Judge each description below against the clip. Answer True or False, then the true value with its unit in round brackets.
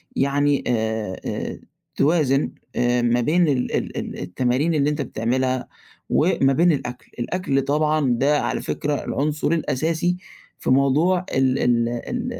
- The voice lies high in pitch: False (140 Hz)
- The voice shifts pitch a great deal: False (3.8 semitones)